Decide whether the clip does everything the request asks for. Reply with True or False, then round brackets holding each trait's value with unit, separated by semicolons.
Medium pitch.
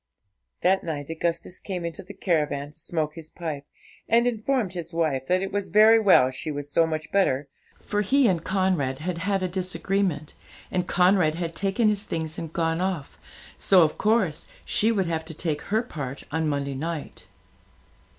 True (170 Hz)